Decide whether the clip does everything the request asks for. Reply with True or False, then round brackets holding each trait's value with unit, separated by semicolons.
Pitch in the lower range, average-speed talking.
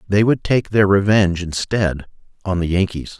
True (95 Hz; 170 wpm)